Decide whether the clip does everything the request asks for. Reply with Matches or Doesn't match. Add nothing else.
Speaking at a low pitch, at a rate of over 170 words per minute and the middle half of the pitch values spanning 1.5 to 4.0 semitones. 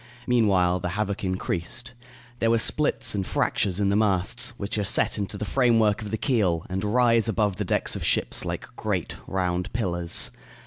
Matches